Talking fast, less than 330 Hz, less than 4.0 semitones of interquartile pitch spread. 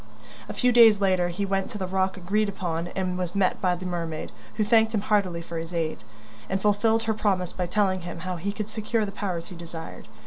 Yes: fast, 230 wpm; high, 190 Hz; average, 3.0 semitones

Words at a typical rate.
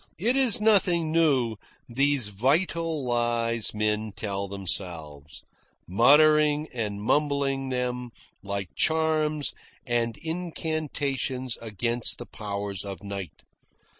No: slow, 100 wpm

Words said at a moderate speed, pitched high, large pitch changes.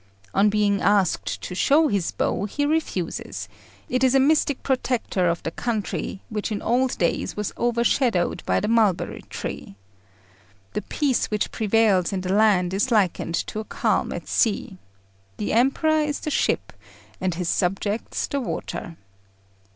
No: average, 155 wpm; high, 215 Hz; average, 5.0 semitones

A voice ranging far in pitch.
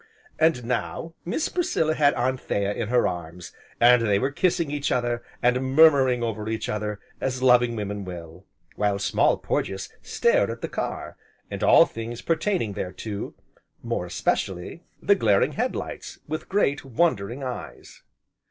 Yes: wide, 5.9 semitones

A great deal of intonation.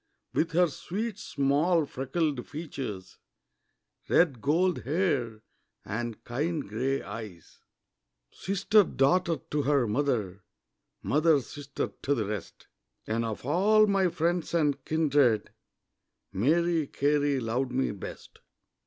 Yes: wide, 5.9 semitones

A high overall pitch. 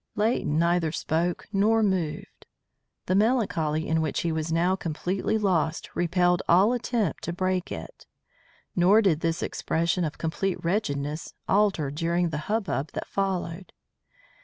No: medium, 175 Hz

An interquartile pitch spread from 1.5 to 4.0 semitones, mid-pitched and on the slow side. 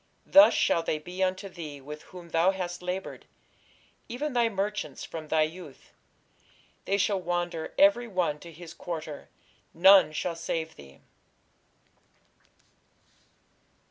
Yes: average, 3.2 semitones; medium, 175 Hz; slow, 125 wpm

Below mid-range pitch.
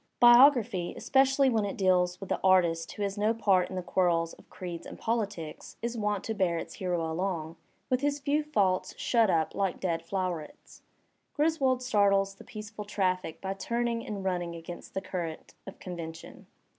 No: high, 195 Hz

